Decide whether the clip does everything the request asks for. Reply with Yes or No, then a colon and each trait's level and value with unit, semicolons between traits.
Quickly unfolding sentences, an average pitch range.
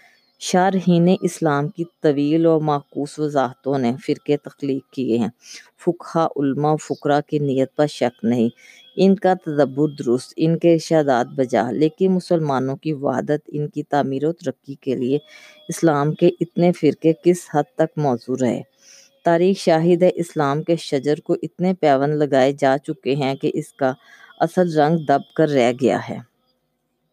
No: average, 155 wpm; average, 3.7 semitones